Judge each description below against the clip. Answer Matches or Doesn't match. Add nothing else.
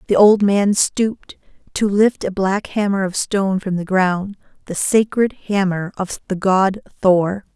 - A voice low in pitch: Doesn't match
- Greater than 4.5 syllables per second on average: Doesn't match